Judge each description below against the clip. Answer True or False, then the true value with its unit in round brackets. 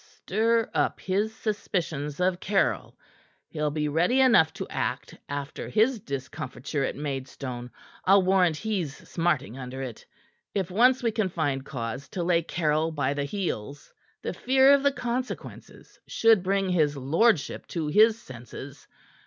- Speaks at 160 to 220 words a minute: False (145 wpm)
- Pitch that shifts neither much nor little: False (6.9 semitones)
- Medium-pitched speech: True (170 Hz)